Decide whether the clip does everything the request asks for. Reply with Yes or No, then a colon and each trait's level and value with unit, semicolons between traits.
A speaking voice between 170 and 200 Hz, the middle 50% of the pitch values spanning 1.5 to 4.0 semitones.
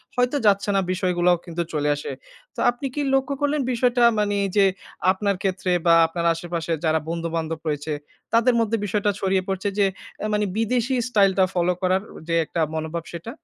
No: high, 190 Hz; average, 4.9 semitones